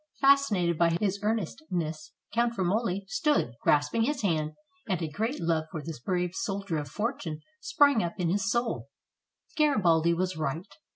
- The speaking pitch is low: No, medium, 185 Hz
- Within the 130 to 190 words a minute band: Yes, average, 155 wpm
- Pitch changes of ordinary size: No, wide, 5.8 semitones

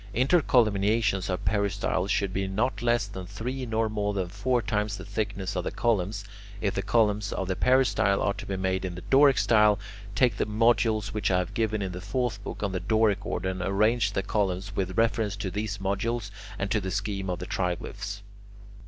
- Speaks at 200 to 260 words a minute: Yes, fast, 205 wpm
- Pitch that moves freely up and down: No, narrow, 2.5 semitones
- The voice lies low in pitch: Yes, low, 100 Hz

